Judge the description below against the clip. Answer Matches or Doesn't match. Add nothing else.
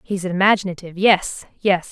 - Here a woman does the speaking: Matches